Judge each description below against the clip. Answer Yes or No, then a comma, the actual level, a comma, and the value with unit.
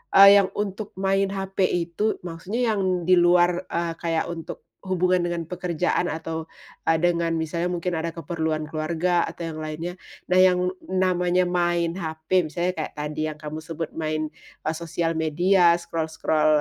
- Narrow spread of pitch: Yes, narrow, 2.2 semitones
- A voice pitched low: No, medium, 170 Hz